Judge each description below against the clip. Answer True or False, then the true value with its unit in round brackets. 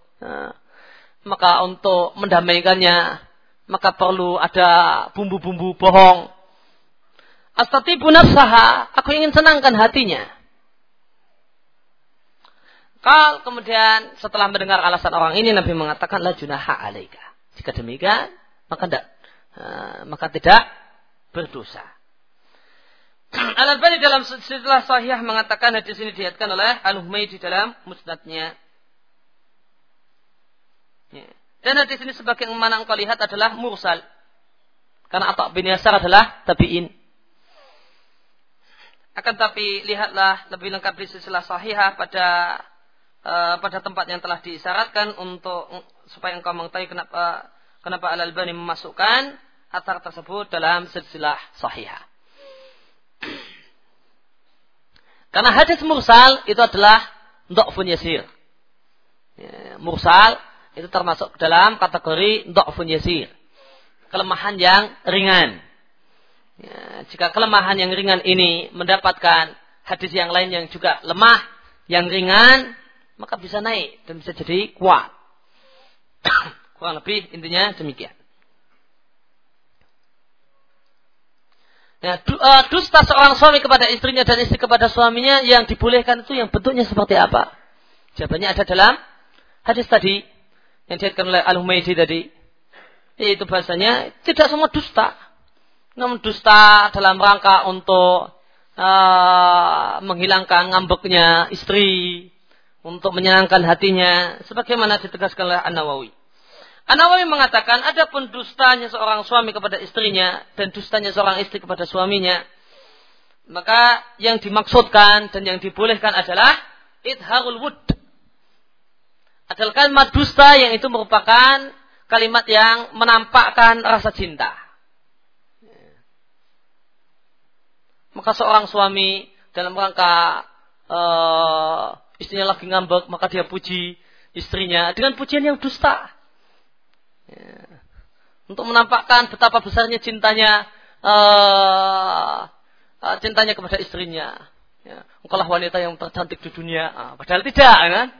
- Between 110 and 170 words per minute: False (100 wpm)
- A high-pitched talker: True (200 Hz)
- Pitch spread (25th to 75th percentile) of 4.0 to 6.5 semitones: True (4.4 semitones)